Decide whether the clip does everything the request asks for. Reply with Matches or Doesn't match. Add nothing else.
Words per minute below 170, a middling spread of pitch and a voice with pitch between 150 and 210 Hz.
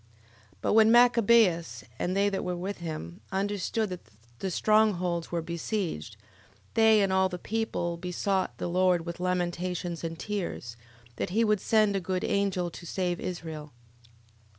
Matches